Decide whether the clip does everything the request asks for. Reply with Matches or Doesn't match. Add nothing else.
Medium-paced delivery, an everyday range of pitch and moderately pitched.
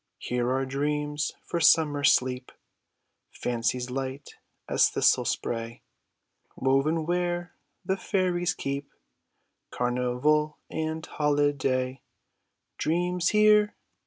Doesn't match